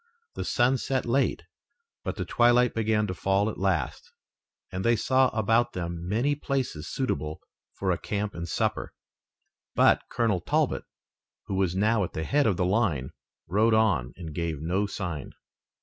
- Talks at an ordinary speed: Yes, average, 165 wpm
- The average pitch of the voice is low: Yes, low, 100 Hz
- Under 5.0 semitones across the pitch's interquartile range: No, average, 5.3 semitones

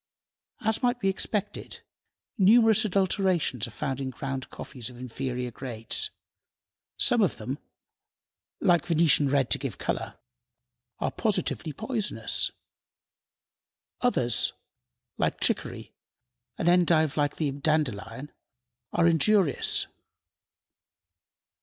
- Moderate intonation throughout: No, wide, 6.6 semitones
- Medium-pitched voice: Yes, medium, 155 Hz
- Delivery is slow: Yes, slow, 100 wpm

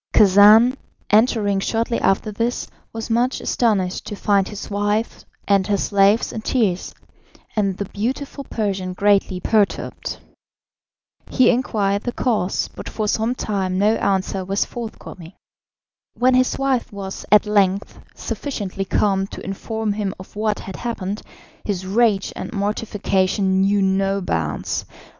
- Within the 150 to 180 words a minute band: No, slow, 135 wpm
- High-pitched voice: Yes, high, 205 Hz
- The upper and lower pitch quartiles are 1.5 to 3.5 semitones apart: Yes, narrow, 2.4 semitones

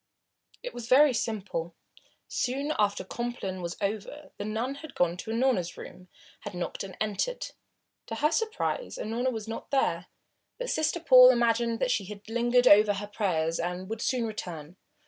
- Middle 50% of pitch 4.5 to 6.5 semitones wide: Yes, average, 4.8 semitones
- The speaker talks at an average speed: Yes, average, 170 wpm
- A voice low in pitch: No, high, 225 Hz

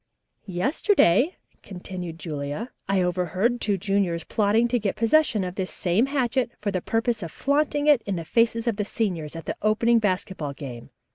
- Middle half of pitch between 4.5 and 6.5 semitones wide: Yes, average, 4.8 semitones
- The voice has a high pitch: Yes, high, 205 Hz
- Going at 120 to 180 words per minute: Yes, average, 170 wpm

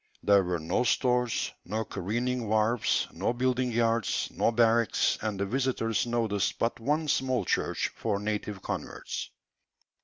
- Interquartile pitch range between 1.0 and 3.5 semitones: Yes, average, 3.1 semitones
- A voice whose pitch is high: No, low, 115 Hz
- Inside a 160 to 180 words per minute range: No, average, 140 wpm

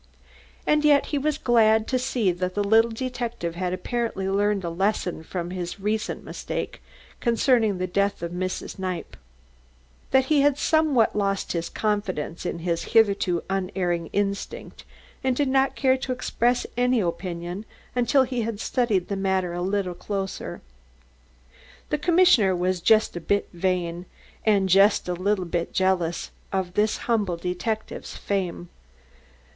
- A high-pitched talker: Yes, high, 200 Hz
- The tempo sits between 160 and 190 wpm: No, average, 150 wpm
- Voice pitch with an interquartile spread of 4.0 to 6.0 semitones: Yes, average, 4.7 semitones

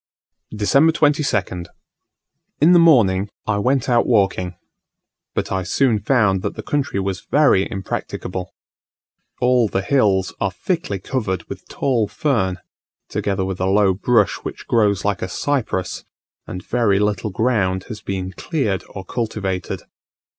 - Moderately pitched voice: No, low, 105 Hz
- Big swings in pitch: No, average, 4.7 semitones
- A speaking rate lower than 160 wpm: Yes, average, 140 wpm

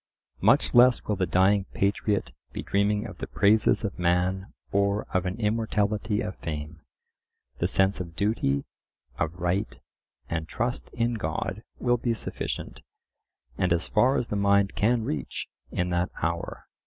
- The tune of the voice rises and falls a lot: No, average, 3.5 semitones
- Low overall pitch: Yes, low, 100 Hz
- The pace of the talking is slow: No, average, 155 wpm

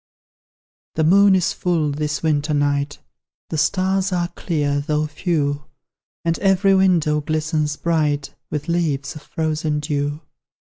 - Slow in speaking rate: Yes, slow, 130 wpm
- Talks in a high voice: No, medium, 155 Hz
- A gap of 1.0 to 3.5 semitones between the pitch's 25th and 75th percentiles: Yes, average, 2.8 semitones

